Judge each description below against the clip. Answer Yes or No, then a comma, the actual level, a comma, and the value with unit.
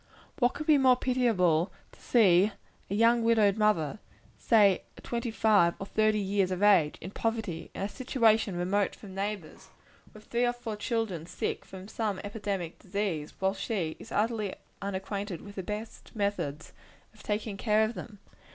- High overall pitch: Yes, high, 205 Hz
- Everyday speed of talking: Yes, average, 170 wpm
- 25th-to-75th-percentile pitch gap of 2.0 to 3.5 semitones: Yes, average, 2.9 semitones